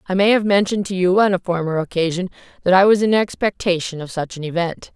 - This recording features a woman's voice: Yes, female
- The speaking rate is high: Yes, fast, 230 wpm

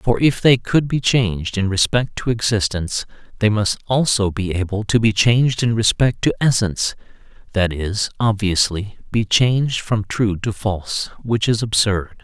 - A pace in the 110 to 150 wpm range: No, average, 160 wpm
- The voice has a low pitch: Yes, low, 105 Hz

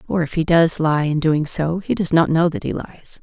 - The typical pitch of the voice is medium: Yes, medium, 160 Hz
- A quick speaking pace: Yes, fast, 280 wpm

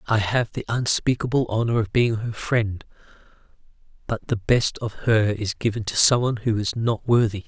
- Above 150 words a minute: Yes, average, 175 wpm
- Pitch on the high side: No, low, 110 Hz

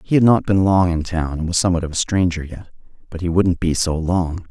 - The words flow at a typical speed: No, fast, 265 wpm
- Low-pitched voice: Yes, very low, 85 Hz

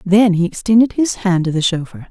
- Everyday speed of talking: No, fast, 230 wpm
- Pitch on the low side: No, high, 190 Hz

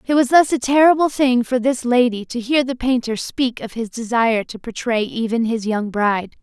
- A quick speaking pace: Yes, fast, 215 wpm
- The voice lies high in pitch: Yes, high, 240 Hz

